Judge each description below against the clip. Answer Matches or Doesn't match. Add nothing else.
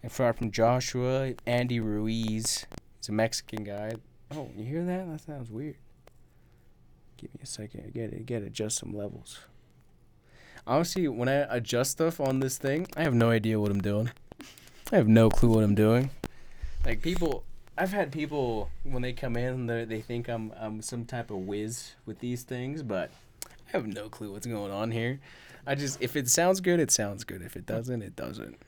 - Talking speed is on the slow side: Doesn't match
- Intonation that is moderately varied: Matches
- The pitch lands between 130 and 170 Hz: Doesn't match